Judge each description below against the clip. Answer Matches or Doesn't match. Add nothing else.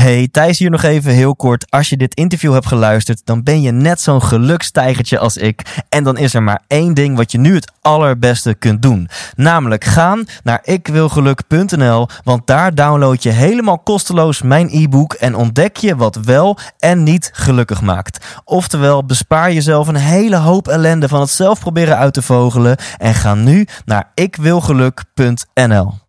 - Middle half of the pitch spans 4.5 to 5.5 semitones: Matches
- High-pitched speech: Doesn't match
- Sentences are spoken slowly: Doesn't match